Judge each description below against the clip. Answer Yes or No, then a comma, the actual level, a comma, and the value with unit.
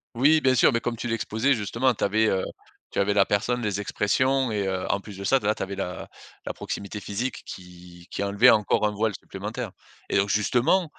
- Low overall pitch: Yes, low, 105 Hz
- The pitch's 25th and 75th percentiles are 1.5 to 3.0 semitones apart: No, average, 3.6 semitones